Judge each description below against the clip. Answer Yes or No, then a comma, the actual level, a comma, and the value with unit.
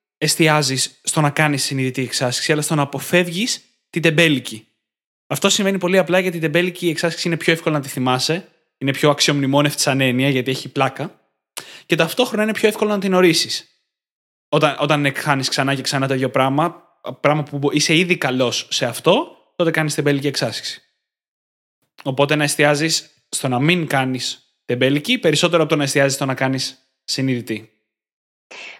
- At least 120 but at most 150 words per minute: No, average, 165 wpm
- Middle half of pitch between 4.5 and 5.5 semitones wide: No, average, 3.9 semitones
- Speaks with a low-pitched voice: No, medium, 145 Hz